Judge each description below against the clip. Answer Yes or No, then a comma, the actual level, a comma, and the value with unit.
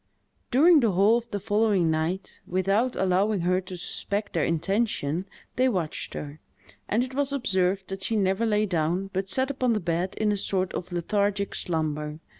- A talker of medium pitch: No, high, 195 Hz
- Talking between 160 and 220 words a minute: Yes, average, 180 wpm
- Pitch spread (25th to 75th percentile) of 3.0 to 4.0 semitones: Yes, average, 3.6 semitones